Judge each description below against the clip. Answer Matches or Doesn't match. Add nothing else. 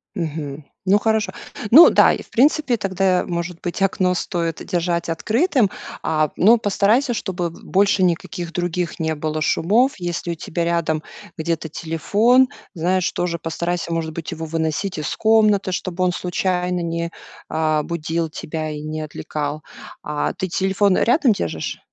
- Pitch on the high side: Doesn't match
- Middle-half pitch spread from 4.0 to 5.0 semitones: Doesn't match